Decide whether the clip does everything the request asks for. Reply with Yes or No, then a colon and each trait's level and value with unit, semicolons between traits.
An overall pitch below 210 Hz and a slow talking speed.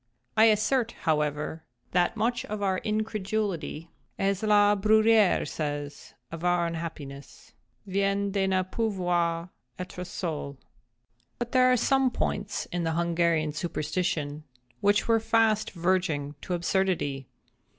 Yes: medium, 185 Hz; slow, 120 wpm